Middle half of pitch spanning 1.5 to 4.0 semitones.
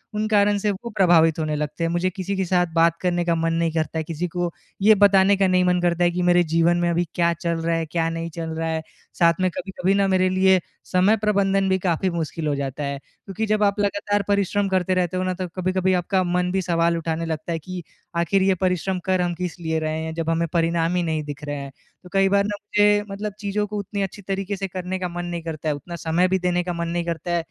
Yes: narrow, 2.5 semitones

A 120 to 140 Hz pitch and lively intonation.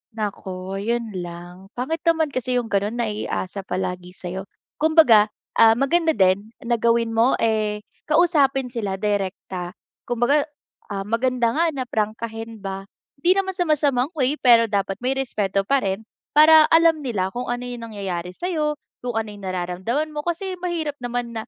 No: high, 230 Hz; wide, 6.2 semitones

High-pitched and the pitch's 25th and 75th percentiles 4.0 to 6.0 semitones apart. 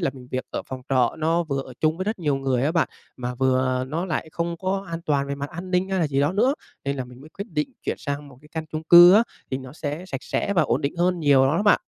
No: medium, 150 Hz; average, 4.3 semitones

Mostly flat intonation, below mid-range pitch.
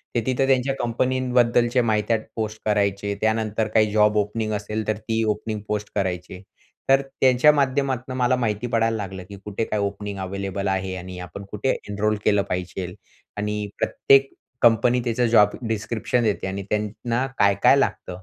No: average, 3.1 semitones; low, 110 Hz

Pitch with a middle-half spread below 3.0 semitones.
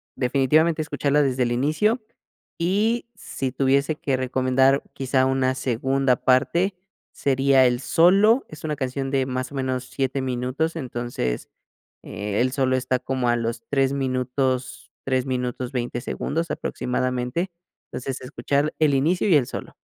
Yes: narrow, 2.4 semitones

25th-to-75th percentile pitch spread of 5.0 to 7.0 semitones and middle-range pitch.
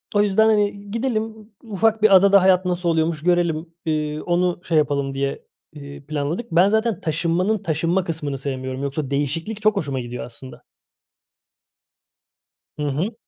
Yes: wide, 5.6 semitones; medium, 170 Hz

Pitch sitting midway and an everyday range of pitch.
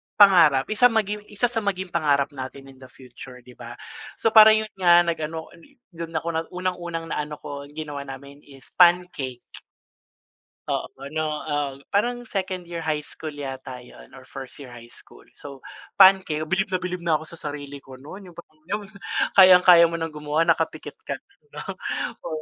Yes: medium, 160 Hz; average, 4.5 semitones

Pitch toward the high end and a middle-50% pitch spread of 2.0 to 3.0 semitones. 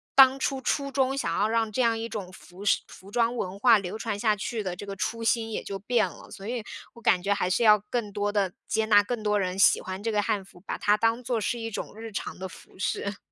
Yes: high, 215 Hz; narrow, 2.6 semitones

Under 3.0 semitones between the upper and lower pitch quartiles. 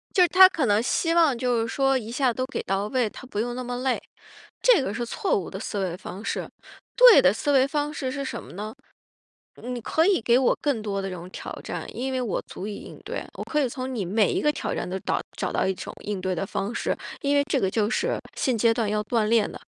No: average, 4.7 semitones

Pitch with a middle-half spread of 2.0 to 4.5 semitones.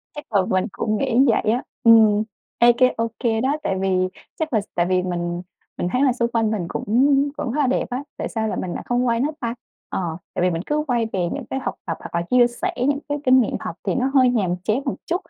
No: average, 5.0 semitones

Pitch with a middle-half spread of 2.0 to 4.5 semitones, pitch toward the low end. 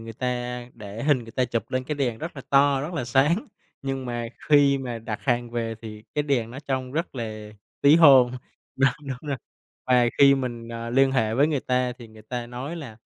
Yes: average, 2.8 semitones; low, 125 Hz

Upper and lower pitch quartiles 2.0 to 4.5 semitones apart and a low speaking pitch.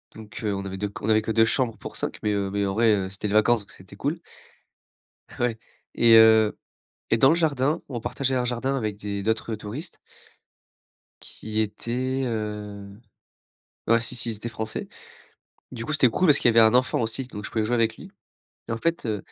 Yes: average, 2.8 semitones; low, 110 Hz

